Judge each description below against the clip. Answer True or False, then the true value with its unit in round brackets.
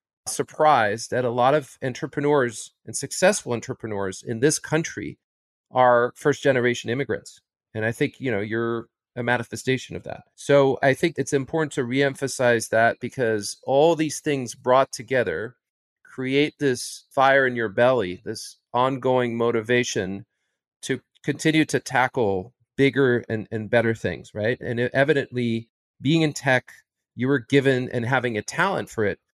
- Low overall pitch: True (125 Hz)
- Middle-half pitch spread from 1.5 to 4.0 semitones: True (3.2 semitones)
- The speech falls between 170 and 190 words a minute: False (150 wpm)